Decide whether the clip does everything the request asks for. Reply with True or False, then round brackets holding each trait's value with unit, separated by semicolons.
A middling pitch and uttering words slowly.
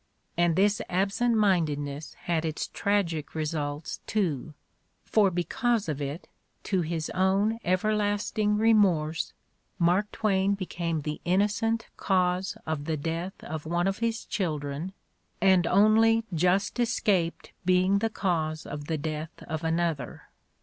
True (180 Hz; 130 wpm)